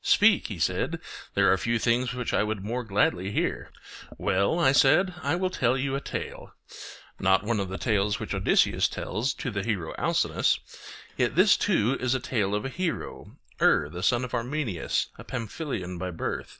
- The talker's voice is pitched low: Yes, low, 115 Hz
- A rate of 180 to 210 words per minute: Yes, average, 190 wpm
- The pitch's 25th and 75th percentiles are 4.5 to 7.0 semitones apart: Yes, average, 5.2 semitones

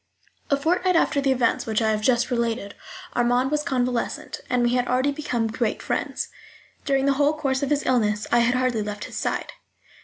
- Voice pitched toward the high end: Yes, very high, 250 Hz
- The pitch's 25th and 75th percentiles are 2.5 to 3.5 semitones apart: Yes, average, 3.0 semitones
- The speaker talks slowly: No, average, 195 wpm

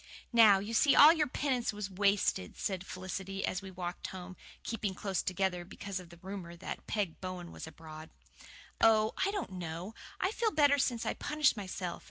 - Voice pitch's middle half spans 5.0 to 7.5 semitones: No, average, 4.0 semitones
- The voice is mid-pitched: No, high, 195 Hz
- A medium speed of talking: Yes, average, 185 wpm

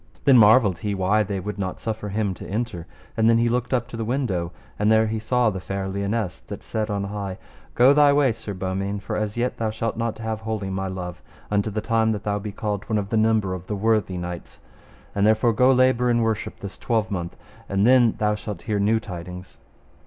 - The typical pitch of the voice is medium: No, low, 105 Hz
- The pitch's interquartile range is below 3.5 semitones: Yes, narrow, 2.5 semitones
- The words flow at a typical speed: No, fast, 225 wpm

